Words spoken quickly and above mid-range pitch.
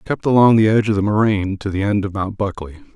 No: fast, 245 wpm; low, 100 Hz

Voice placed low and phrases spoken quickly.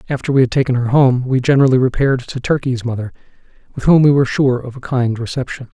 Yes: low, 130 Hz; fast, 220 wpm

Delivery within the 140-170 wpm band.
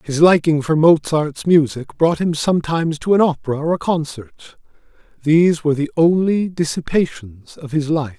Yes: average, 160 wpm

